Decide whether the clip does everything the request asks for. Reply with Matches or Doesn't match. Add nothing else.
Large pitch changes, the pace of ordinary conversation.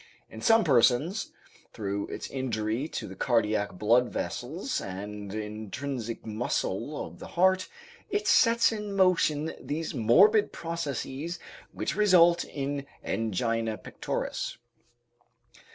Doesn't match